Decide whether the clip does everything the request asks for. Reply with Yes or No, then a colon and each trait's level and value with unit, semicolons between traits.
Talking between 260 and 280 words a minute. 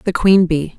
No: fast, 230 wpm